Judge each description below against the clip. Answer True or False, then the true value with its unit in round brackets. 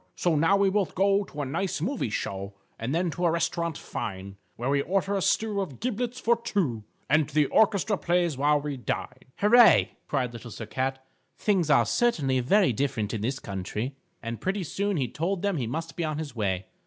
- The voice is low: False (155 Hz)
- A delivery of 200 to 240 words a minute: True (205 wpm)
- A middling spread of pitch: False (7.5 semitones)